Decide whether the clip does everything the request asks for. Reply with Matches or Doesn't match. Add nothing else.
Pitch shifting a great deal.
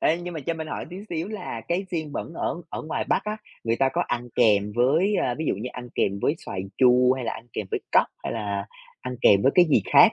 Matches